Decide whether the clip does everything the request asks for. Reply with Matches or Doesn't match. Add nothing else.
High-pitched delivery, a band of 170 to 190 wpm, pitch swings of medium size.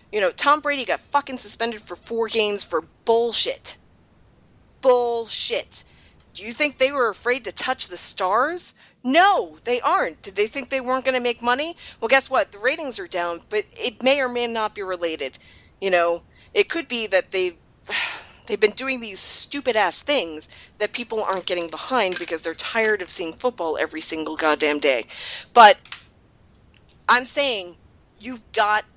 Doesn't match